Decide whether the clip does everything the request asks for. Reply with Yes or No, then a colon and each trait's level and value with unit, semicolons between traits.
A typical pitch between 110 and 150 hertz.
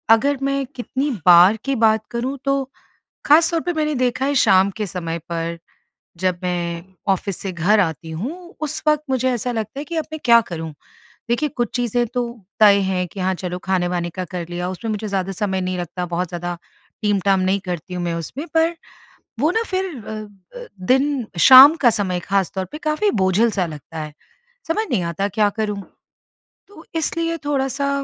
No: high, 210 Hz